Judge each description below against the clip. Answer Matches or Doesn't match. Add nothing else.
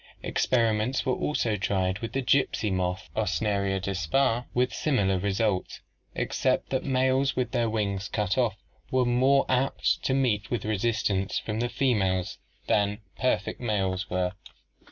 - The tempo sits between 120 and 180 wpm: Matches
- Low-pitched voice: Matches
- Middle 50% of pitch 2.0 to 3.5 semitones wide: Doesn't match